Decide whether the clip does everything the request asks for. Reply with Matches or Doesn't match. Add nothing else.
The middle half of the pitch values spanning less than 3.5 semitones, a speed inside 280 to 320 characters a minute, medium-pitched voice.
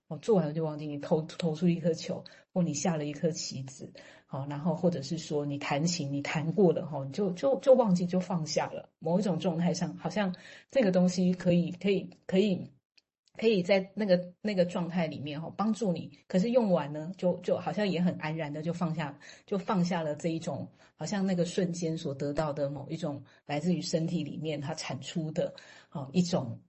Matches